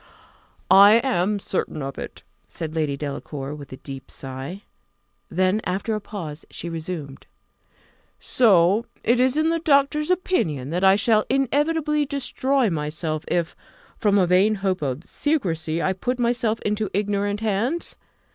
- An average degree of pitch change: No, wide, 7.3 semitones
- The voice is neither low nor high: No, high, 200 Hz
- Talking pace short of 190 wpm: Yes, average, 140 wpm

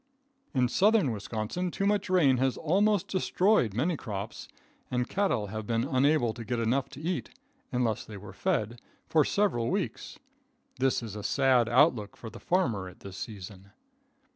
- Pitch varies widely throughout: Yes, wide, 7.8 semitones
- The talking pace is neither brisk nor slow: Yes, average, 165 wpm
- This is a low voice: Yes, low, 125 Hz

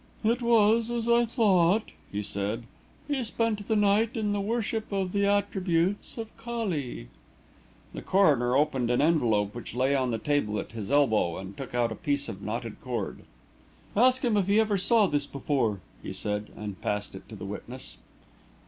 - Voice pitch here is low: No, medium, 170 Hz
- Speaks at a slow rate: No, average, 180 wpm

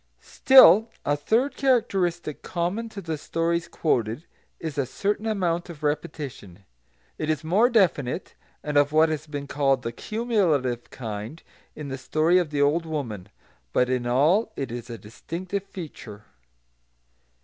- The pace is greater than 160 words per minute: No, average, 150 wpm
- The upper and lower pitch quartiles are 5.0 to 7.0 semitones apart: Yes, wide, 5.4 semitones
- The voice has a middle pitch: Yes, medium, 155 Hz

